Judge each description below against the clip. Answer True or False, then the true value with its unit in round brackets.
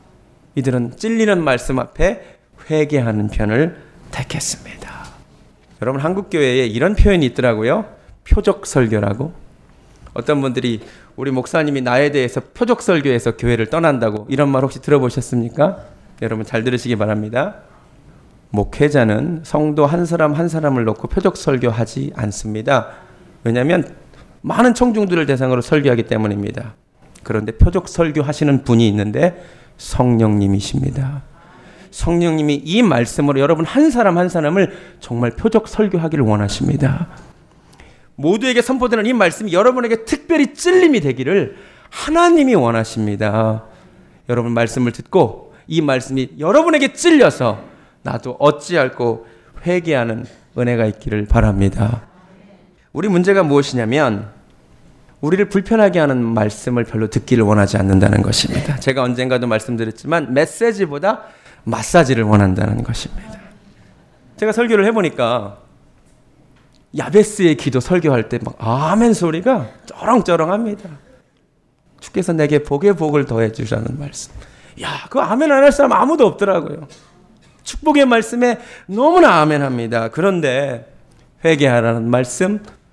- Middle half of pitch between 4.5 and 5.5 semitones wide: False (7.7 semitones)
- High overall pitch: False (145 Hz)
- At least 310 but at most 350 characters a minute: True (315 characters per minute)